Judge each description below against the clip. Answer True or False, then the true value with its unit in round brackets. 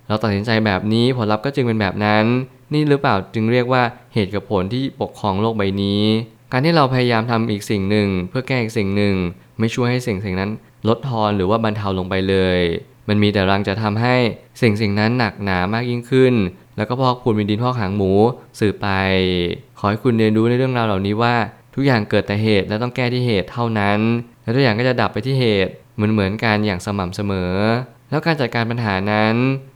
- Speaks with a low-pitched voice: True (110 Hz)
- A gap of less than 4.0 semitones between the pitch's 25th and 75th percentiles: True (3.3 semitones)